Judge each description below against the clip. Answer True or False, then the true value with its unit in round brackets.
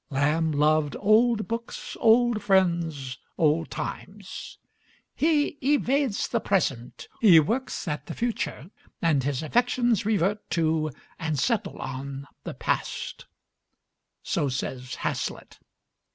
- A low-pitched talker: False (170 Hz)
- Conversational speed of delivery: False (110 wpm)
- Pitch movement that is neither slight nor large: False (7.6 semitones)